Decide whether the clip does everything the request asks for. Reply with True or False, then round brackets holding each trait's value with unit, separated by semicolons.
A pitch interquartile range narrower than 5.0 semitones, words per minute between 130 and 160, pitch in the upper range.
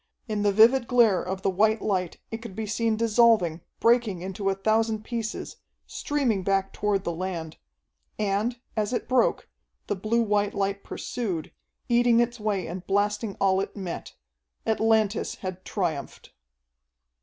True (2.9 semitones; 150 wpm; 210 Hz)